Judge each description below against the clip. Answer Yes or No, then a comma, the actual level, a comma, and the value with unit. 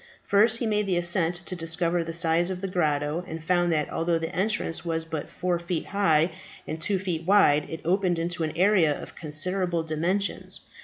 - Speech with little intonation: Yes, narrow, 2.3 semitones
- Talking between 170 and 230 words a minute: Yes, average, 195 wpm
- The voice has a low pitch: No, medium, 170 Hz